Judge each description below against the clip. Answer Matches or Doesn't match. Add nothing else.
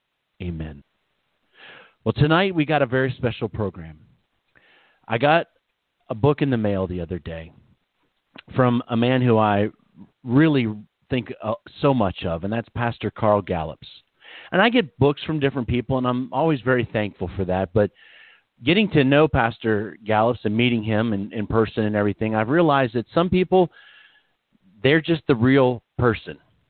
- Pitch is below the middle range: Matches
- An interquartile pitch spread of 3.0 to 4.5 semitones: Doesn't match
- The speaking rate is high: Doesn't match